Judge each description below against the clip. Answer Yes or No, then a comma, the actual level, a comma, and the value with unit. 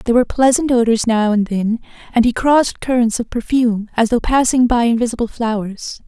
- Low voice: No, high, 235 Hz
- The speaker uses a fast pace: No, average, 190 wpm